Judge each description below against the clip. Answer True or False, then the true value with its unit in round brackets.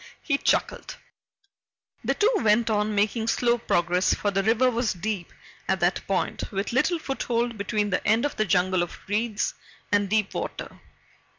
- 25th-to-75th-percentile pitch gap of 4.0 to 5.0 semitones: False (3.3 semitones)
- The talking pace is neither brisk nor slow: True (165 wpm)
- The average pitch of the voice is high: True (215 Hz)